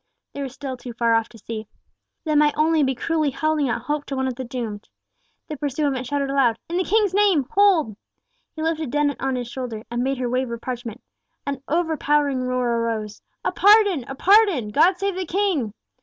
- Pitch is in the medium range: No, very high, 275 Hz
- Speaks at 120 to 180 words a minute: No, average, 200 wpm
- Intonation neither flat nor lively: Yes, average, 4.6 semitones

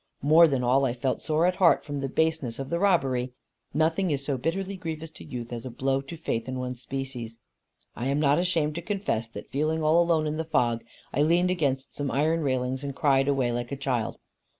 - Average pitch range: Yes, average, 3.9 semitones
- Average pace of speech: No, fast, 220 wpm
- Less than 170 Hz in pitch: Yes, medium, 140 Hz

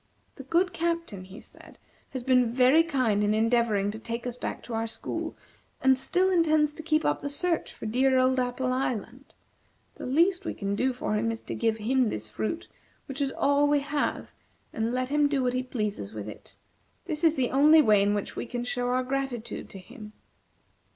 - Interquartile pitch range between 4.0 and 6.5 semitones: Yes, average, 4.3 semitones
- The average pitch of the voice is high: Yes, very high, 255 Hz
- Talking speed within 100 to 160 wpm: No, fast, 205 wpm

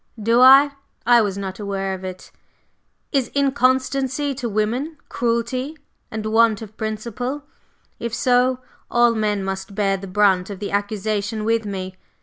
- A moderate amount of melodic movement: Yes, average, 3.9 semitones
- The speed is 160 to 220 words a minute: No, average, 145 wpm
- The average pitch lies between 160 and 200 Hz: No, high, 220 Hz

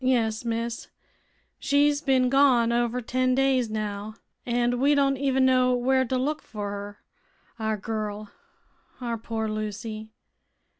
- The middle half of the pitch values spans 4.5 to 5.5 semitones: No, average, 3.1 semitones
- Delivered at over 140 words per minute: No, slow, 135 wpm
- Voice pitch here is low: No, high, 240 Hz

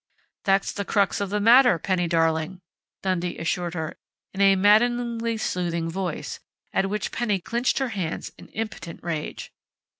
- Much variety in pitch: No, average, 4.2 semitones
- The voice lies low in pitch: No, high, 195 Hz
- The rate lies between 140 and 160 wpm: Yes, average, 150 wpm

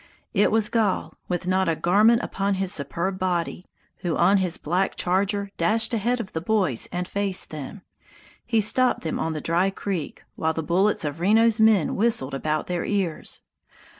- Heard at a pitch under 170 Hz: No, high, 190 Hz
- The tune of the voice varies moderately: Yes, average, 3.7 semitones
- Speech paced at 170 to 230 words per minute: Yes, average, 175 wpm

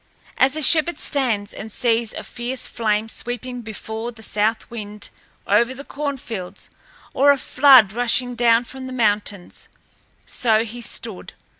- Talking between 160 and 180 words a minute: No, average, 150 wpm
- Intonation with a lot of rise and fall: No, average, 3.0 semitones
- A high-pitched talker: Yes, high, 235 Hz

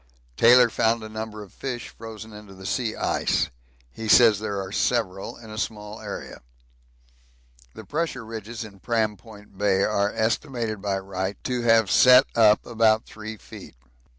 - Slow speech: No, average, 160 wpm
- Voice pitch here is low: Yes, low, 110 Hz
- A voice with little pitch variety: Yes, narrow, 2.0 semitones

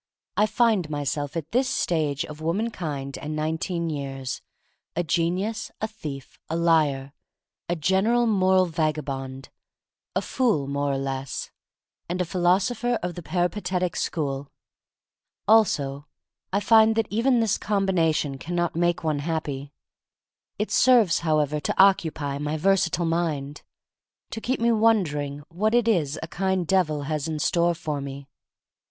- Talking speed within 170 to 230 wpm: No, average, 145 wpm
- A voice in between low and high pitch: Yes, medium, 165 Hz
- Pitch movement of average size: Yes, average, 4.9 semitones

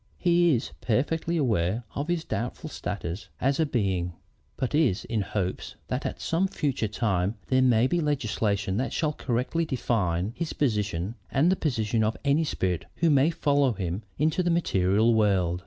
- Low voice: Yes, low, 120 Hz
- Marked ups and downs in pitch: Yes, wide, 6.9 semitones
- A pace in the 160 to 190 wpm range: Yes, average, 170 wpm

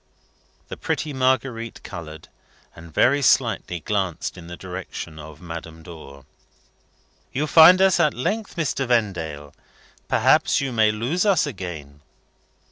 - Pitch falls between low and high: No, low, 100 Hz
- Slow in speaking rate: Yes, slow, 125 wpm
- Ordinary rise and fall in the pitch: No, wide, 8.7 semitones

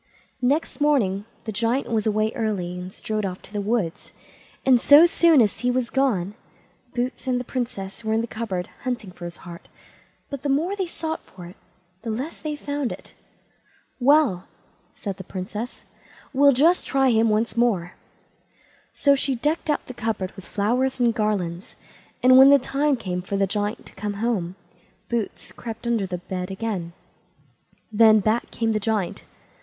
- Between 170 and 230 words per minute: Yes, average, 175 wpm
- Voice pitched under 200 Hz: No, high, 225 Hz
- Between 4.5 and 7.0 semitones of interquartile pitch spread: Yes, average, 4.8 semitones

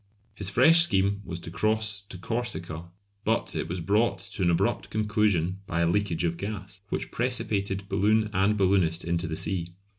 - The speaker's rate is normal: Yes, average, 175 wpm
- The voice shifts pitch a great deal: No, average, 3.6 semitones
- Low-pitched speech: Yes, very low, 95 Hz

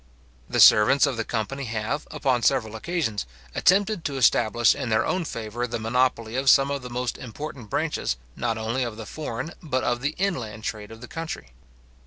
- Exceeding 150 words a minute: Yes, average, 190 wpm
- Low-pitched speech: Yes, low, 125 Hz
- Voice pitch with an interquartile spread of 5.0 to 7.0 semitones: No, average, 3.9 semitones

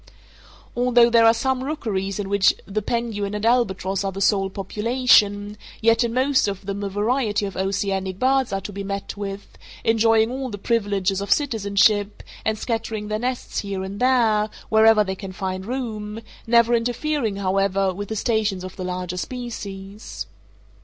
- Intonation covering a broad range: No, average, 3.0 semitones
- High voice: Yes, high, 210 Hz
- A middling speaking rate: Yes, average, 165 wpm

